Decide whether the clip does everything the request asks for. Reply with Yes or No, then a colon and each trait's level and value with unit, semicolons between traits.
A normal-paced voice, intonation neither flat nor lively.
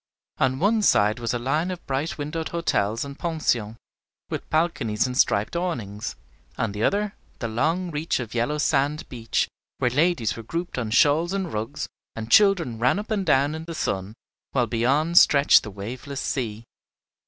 No: average, 175 wpm; wide, 6.5 semitones